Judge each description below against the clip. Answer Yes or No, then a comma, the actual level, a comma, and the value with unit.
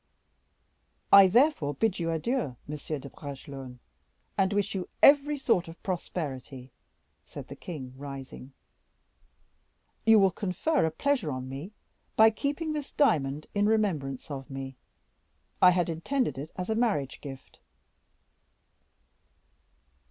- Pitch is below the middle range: No, medium, 170 Hz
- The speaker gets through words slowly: Yes, slow, 125 wpm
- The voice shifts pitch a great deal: Yes, wide, 8.1 semitones